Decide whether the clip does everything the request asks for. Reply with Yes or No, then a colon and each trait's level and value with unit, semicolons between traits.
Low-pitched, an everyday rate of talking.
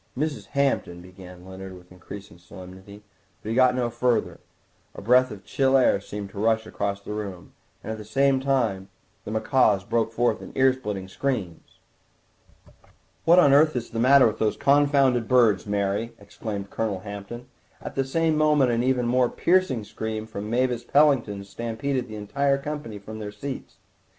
Yes: low, 115 Hz; average, 170 wpm